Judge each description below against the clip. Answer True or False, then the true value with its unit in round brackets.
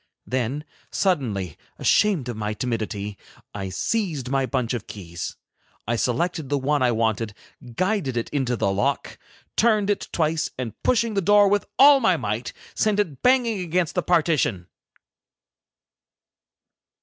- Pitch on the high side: False (135 Hz)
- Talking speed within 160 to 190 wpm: False (140 wpm)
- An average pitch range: False (8.9 semitones)